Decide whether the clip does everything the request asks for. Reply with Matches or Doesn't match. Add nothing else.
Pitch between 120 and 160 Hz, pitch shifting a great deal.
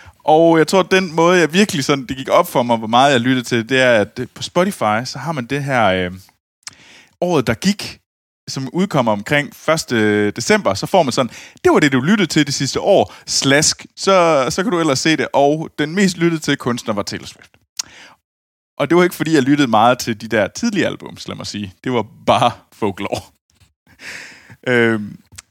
Matches